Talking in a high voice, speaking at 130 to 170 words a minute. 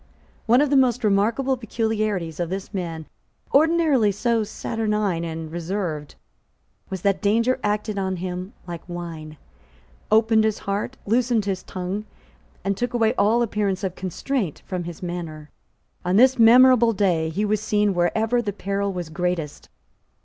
Yes: high, 200 Hz; average, 150 wpm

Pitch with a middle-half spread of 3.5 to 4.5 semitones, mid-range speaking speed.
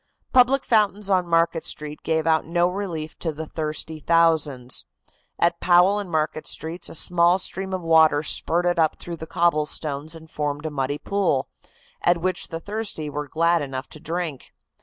No: narrow, 2.5 semitones; average, 170 wpm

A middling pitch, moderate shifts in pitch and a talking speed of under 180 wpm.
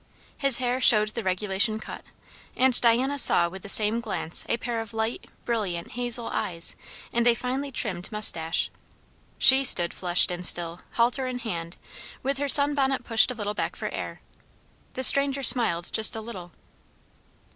No: high, 230 Hz; average, 4.9 semitones; average, 170 wpm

